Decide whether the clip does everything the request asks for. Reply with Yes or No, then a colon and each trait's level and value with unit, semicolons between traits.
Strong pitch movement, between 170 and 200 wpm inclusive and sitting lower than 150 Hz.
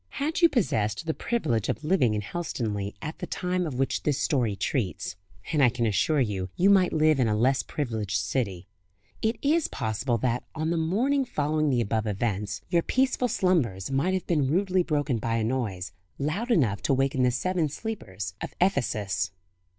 Yes: wide, 8.2 semitones; average, 185 wpm; low, 135 Hz